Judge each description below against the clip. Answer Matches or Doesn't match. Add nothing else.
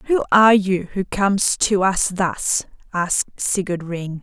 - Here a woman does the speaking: Matches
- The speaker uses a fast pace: Doesn't match